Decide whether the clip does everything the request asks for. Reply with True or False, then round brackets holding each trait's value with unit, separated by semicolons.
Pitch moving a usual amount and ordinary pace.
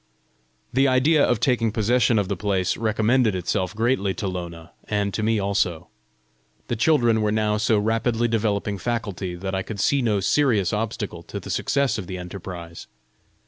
True (3.6 semitones; 170 wpm)